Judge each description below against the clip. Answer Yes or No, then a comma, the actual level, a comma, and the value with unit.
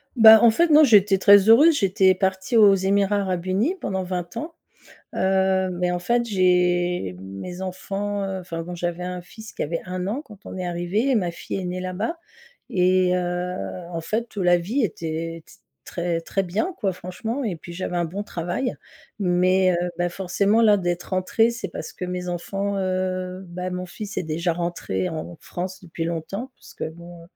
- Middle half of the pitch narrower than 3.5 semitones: Yes, narrow, 2.4 semitones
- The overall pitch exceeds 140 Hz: Yes, medium, 185 Hz